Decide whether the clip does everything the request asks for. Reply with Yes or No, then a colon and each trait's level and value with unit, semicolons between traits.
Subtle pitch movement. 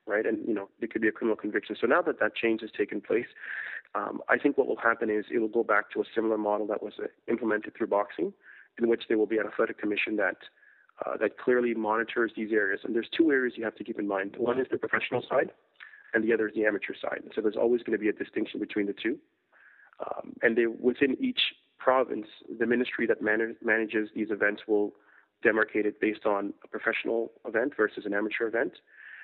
Yes: narrow, 1.6 semitones